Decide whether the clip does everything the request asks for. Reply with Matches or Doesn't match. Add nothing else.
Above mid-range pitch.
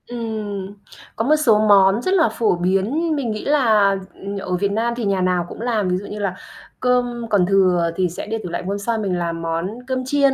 Matches